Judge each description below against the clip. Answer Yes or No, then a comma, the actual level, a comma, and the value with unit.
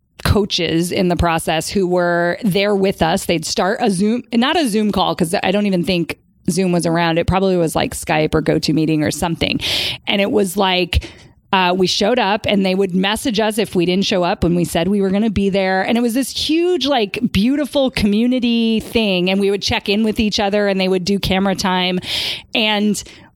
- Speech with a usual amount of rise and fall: Yes, average, 3.2 semitones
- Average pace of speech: No, fast, 225 wpm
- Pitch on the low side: No, high, 195 Hz